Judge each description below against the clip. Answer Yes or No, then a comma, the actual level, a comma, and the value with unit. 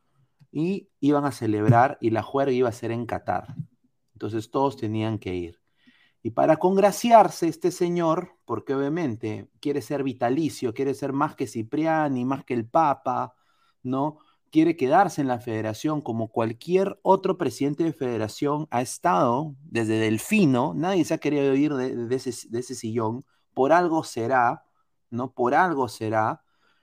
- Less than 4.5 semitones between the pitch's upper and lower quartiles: No, average, 4.9 semitones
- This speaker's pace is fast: No, average, 160 wpm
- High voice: No, low, 135 Hz